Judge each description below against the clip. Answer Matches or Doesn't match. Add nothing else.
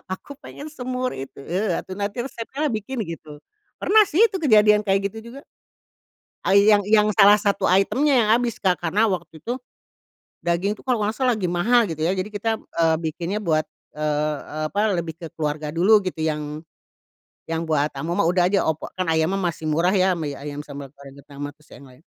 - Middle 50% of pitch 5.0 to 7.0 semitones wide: Matches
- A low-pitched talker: Doesn't match